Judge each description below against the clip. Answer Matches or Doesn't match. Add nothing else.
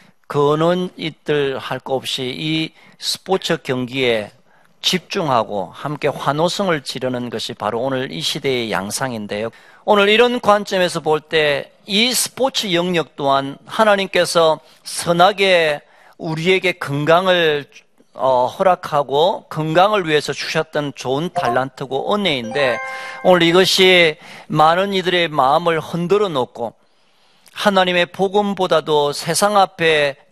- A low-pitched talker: Doesn't match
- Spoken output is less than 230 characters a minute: Doesn't match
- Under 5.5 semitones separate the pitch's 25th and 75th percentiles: Matches